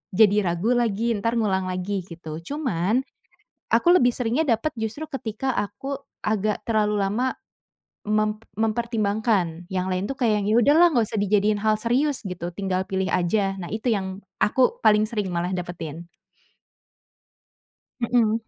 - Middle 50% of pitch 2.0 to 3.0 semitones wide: No, average, 3.7 semitones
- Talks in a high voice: Yes, high, 215 Hz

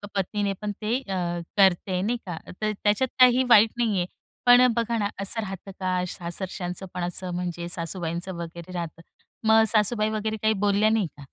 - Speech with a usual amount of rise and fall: Yes, average, 3.5 semitones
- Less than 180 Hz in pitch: No, high, 195 Hz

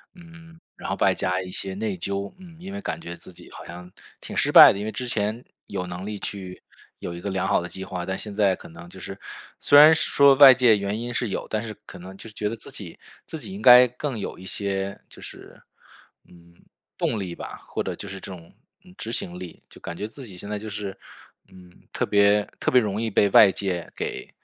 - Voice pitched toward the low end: Yes, low, 100 Hz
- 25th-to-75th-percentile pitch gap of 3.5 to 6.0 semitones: Yes, average, 4.1 semitones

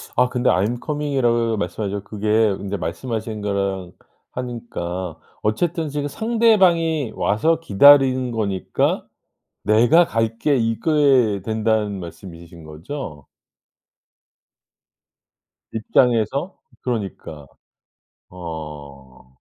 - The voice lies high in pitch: No, low, 110 Hz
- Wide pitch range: Yes, wide, 6.1 semitones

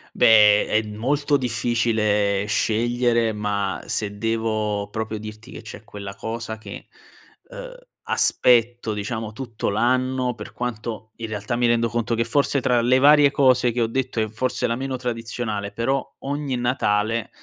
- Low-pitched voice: Yes, low, 115 Hz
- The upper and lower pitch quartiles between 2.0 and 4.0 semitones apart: Yes, narrow, 2.5 semitones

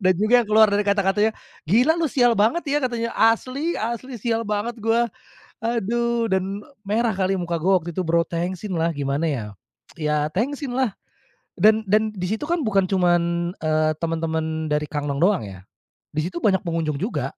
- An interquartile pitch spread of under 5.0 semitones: No, wide, 5.5 semitones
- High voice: Yes, high, 195 Hz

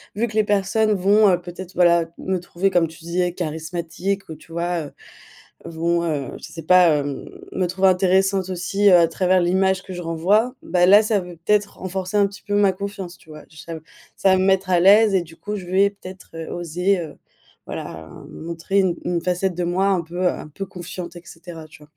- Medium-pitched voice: Yes, medium, 180 Hz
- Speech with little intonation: Yes, narrow, 2.3 semitones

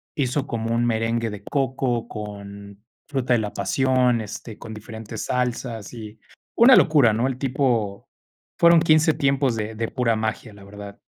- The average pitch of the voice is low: Yes, low, 115 Hz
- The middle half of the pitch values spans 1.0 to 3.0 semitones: No, average, 3.5 semitones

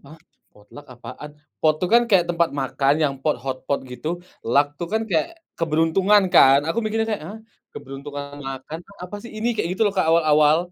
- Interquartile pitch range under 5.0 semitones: No, wide, 5.5 semitones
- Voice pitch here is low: No, medium, 155 Hz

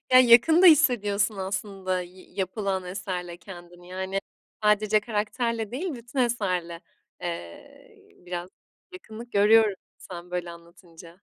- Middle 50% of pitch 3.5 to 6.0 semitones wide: Yes, average, 4.0 semitones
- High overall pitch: Yes, high, 195 Hz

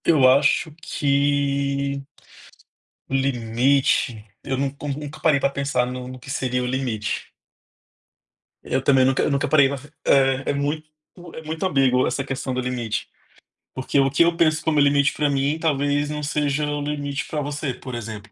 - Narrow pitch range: Yes, narrow, 1.9 semitones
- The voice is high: No, medium, 140 Hz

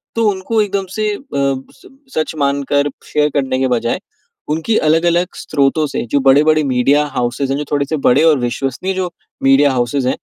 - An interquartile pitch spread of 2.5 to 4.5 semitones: Yes, average, 3.3 semitones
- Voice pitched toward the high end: No, medium, 145 Hz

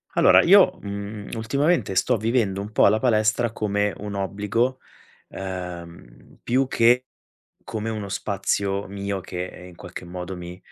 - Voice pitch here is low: Yes, low, 100 Hz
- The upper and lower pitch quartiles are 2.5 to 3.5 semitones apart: Yes, average, 2.8 semitones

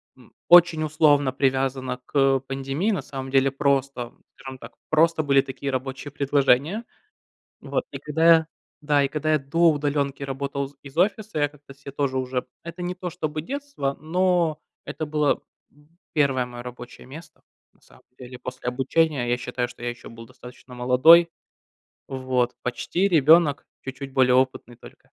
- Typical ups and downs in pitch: Yes, average, 3.2 semitones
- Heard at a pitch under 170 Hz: Yes, medium, 140 Hz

